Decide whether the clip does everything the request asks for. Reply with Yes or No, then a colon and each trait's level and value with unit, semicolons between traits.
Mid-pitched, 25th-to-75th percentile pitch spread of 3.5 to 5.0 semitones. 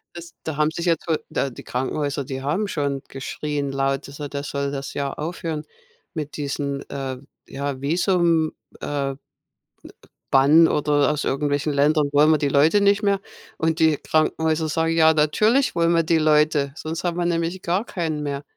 No: medium, 150 Hz; average, 2.7 semitones